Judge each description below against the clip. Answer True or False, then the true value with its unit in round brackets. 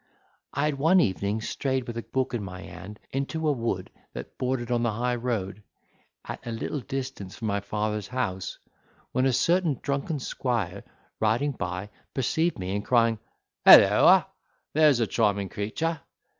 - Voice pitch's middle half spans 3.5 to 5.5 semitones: True (4.8 semitones)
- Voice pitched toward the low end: True (120 Hz)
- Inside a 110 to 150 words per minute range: False (160 wpm)